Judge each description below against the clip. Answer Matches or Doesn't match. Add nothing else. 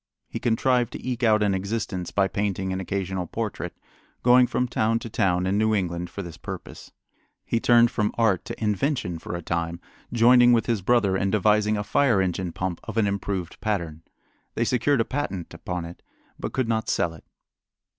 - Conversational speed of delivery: Matches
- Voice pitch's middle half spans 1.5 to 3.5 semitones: Doesn't match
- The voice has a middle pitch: Doesn't match